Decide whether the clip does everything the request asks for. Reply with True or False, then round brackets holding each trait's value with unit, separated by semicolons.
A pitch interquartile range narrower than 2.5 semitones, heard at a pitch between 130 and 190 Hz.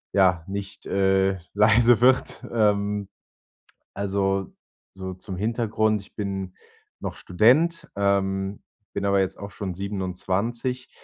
False (2.0 semitones; 100 Hz)